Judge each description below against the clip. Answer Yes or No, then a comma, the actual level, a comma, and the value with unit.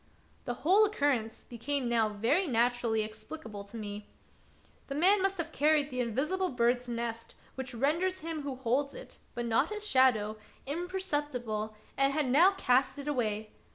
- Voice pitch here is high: Yes, very high, 260 Hz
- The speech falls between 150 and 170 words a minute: Yes, average, 160 wpm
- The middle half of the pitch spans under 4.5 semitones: No, average, 5.1 semitones